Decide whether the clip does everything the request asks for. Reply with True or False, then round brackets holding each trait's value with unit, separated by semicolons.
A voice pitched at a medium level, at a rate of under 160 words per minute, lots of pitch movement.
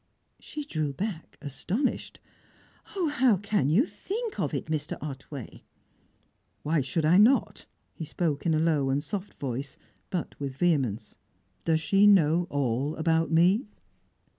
True (160 Hz; 140 wpm; 5.8 semitones)